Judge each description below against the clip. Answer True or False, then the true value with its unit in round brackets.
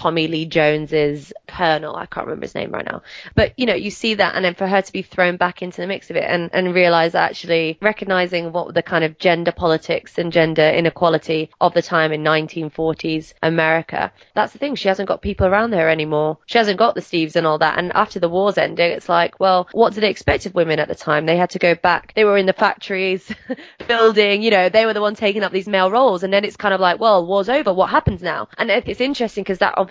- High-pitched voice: False (180 Hz)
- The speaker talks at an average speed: False (250 wpm)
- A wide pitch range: False (3.7 semitones)